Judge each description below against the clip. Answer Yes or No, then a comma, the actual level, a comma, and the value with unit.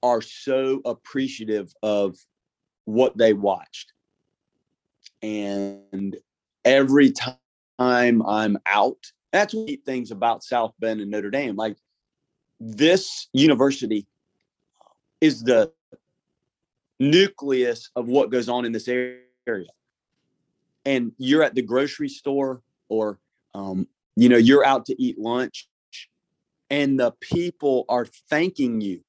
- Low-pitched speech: Yes, low, 125 Hz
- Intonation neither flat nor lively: Yes, average, 4.1 semitones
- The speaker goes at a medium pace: No, slow, 115 wpm